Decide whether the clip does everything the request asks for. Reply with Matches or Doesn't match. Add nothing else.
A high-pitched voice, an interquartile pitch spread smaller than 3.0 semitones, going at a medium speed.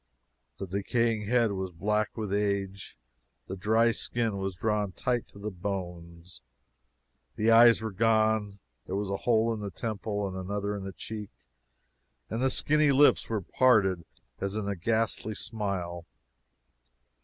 Doesn't match